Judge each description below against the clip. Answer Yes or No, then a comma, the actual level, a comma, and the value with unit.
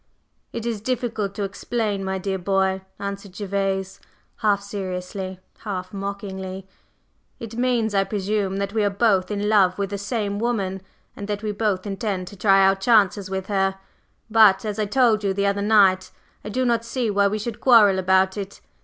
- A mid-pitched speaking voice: No, high, 200 Hz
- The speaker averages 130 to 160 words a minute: No, average, 180 wpm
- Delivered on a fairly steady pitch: Yes, narrow, 1.9 semitones